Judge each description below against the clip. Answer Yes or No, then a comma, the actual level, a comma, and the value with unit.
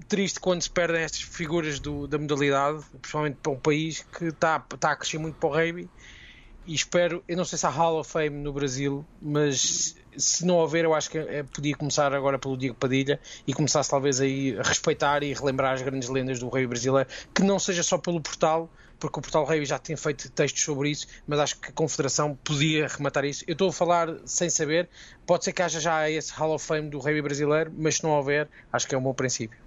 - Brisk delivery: Yes, fast, 235 wpm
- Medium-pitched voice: Yes, medium, 150 Hz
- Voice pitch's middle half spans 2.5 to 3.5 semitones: Yes, average, 2.8 semitones